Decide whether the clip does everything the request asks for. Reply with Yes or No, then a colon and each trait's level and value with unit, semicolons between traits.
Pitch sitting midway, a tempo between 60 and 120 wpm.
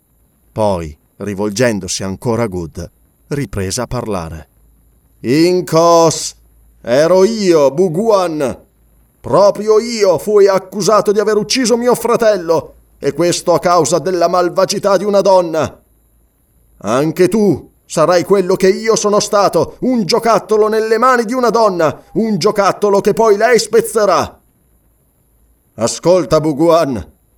Yes: medium, 180 Hz; slow, 115 wpm